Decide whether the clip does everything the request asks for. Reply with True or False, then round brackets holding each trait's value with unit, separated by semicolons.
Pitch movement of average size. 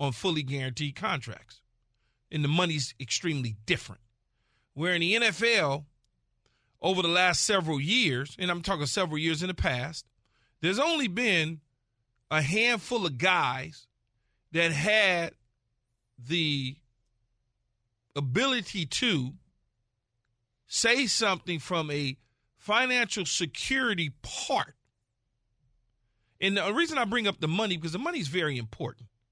False (7.3 semitones)